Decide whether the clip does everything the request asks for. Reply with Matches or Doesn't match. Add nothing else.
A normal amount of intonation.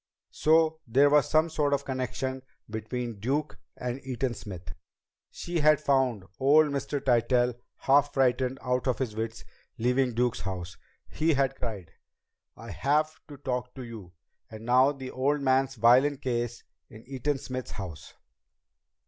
Matches